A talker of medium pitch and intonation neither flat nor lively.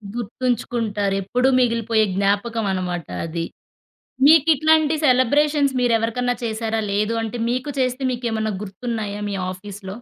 No: high, 230 Hz; average, 3.6 semitones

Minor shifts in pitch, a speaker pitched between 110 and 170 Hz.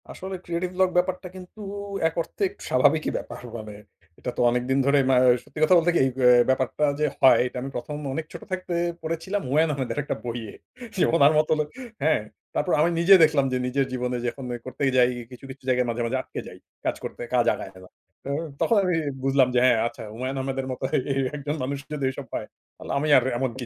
No: average, 4.1 semitones; low, 135 Hz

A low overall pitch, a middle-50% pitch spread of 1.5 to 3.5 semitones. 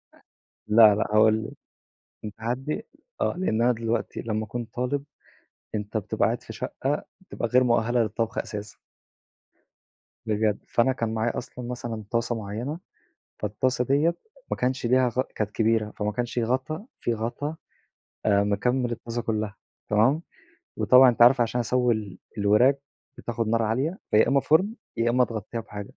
Yes: low, 115 Hz; average, 2.7 semitones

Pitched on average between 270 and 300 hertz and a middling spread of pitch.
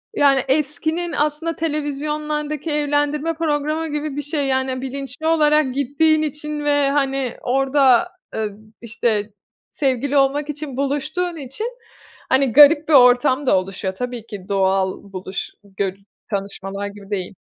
Yes: very high, 280 Hz; average, 3.5 semitones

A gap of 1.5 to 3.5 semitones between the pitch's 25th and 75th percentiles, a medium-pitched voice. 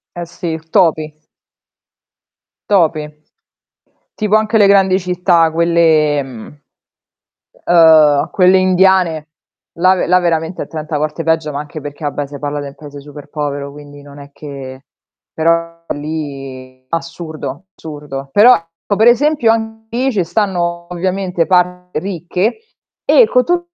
No: average, 4.0 semitones; medium, 165 Hz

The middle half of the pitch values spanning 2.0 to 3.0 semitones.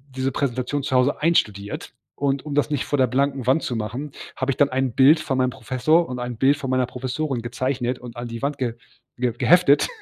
Yes: narrow, 2.4 semitones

